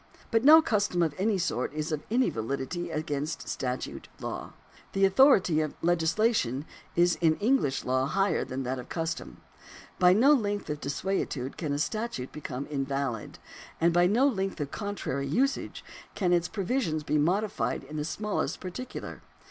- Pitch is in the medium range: Yes, medium, 170 Hz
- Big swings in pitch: Yes, wide, 6.2 semitones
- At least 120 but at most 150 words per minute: No, average, 165 wpm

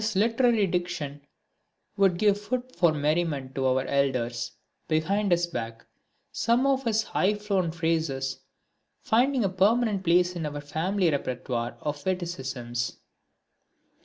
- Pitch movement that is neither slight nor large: No, wide, 6.8 semitones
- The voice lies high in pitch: No, medium, 175 Hz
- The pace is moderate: No, slow, 130 wpm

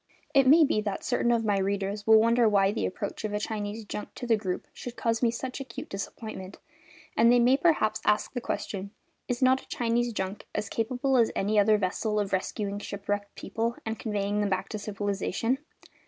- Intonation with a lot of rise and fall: No, average, 2.8 semitones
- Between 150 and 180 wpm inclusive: No, average, 200 wpm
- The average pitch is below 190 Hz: No, high, 215 Hz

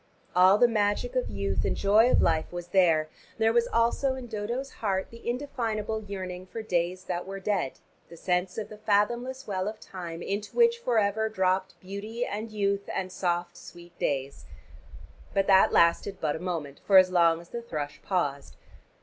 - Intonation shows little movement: No, average, 3.9 semitones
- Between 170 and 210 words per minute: Yes, average, 185 wpm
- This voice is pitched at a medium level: No, high, 195 Hz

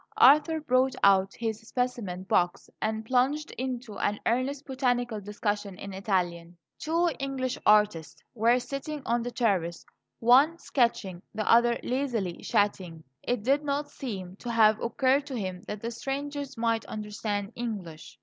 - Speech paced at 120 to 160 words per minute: Yes, average, 145 wpm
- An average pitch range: Yes, average, 4.4 semitones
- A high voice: Yes, high, 230 Hz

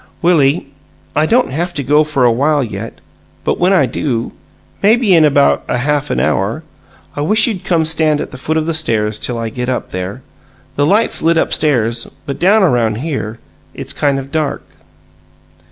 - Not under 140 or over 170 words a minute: No, average, 190 wpm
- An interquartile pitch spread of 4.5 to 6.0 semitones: Yes, average, 5.0 semitones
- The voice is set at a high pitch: No, medium, 145 Hz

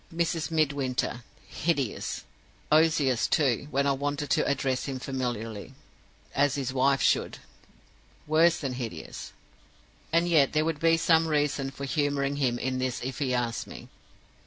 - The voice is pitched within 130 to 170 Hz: Yes, medium, 140 Hz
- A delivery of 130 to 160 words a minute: Yes, average, 145 wpm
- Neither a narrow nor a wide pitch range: Yes, average, 3.0 semitones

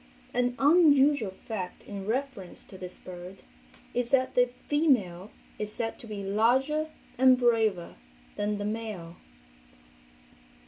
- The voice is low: No, high, 225 Hz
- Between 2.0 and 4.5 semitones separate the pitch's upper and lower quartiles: No, average, 5.0 semitones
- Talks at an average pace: No, slow, 125 wpm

